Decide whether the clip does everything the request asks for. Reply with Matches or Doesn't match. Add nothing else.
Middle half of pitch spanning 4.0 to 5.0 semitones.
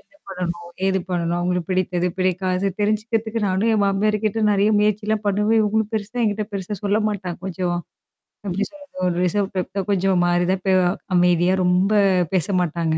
Doesn't match